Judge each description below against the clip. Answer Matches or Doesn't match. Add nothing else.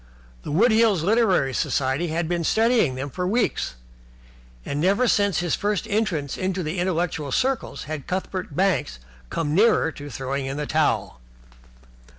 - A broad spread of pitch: Matches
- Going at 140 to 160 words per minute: Matches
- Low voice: Doesn't match